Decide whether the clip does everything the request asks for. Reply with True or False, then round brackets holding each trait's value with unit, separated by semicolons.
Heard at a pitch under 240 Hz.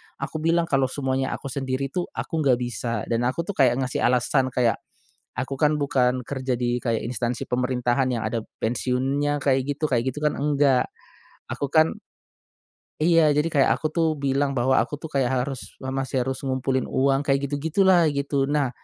True (135 Hz)